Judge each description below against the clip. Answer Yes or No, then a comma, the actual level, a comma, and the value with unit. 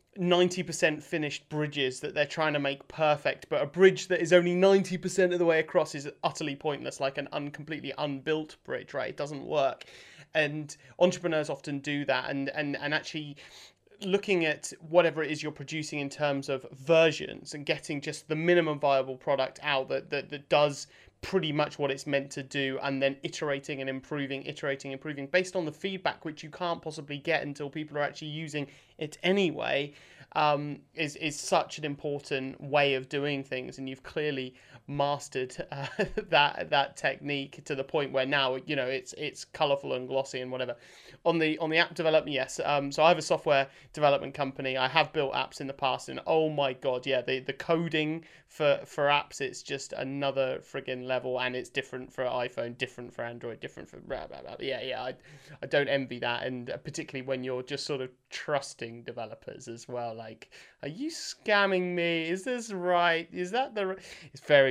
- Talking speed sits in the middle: Yes, average, 195 wpm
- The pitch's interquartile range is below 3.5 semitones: Yes, average, 3.0 semitones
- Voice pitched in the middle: Yes, medium, 145 Hz